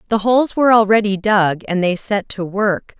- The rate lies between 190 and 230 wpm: Yes, average, 200 wpm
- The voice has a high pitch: Yes, high, 205 Hz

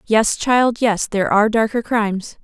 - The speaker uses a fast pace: No, average, 170 wpm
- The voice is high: Yes, high, 220 Hz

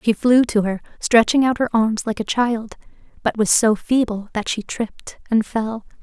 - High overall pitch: Yes, high, 225 Hz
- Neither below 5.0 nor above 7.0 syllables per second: No, 4.6 syllables/s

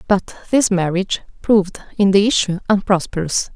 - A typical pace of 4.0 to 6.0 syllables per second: Yes, 5.3 syllables/s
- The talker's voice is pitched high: Yes, high, 195 Hz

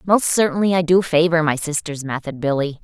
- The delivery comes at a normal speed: Yes, average, 190 wpm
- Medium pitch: Yes, medium, 165 Hz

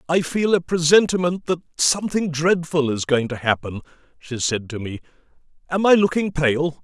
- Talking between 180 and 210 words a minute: No, average, 165 wpm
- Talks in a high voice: No, medium, 160 Hz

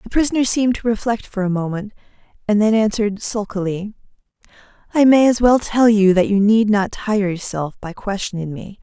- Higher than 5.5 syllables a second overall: No, 5.4 syllables/s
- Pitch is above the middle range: Yes, high, 210 Hz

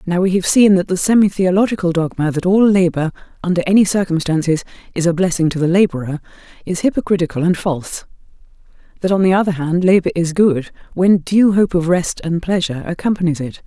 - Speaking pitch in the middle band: Yes, medium, 180 Hz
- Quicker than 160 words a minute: Yes, average, 185 wpm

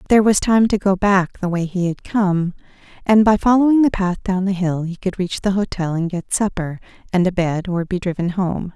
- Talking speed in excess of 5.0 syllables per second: Yes, 5.2 syllables/s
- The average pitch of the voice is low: No, high, 190 Hz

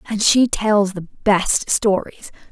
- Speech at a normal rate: Yes, average, 145 wpm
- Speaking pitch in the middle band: No, high, 205 Hz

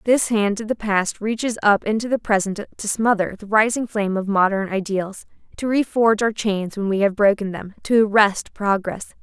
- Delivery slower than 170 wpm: No, average, 195 wpm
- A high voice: Yes, high, 210 Hz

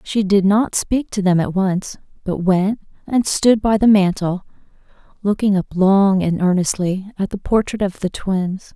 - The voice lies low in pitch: No, high, 195 Hz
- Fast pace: No, average, 180 wpm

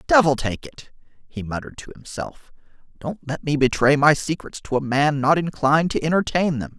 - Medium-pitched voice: Yes, medium, 145 Hz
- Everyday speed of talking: Yes, average, 185 wpm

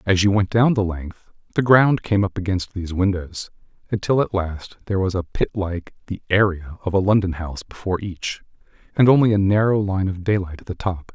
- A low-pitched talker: Yes, very low, 95 Hz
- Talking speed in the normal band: No, fast, 210 wpm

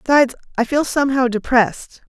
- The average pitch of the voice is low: No, very high, 255 Hz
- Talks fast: No, average, 140 wpm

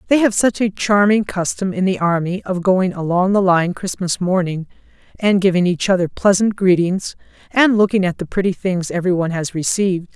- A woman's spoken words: Yes, female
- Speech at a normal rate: Yes, average, 185 wpm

